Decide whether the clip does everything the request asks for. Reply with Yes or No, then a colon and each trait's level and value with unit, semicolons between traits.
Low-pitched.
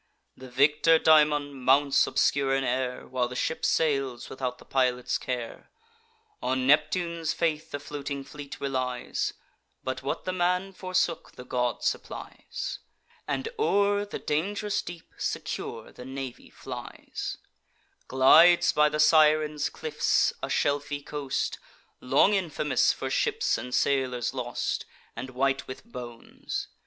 No: medium, 145 Hz